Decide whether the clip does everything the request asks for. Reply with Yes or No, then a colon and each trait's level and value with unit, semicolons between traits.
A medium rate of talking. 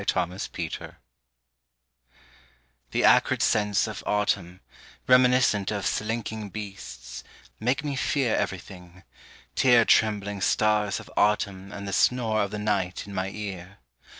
No: slow, 125 wpm